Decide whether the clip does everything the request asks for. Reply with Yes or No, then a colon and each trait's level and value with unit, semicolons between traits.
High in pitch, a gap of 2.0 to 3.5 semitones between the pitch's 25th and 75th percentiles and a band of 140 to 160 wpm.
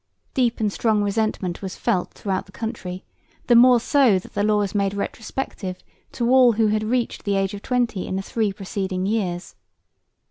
No: high, 210 Hz; average, 3.2 semitones; average, 185 wpm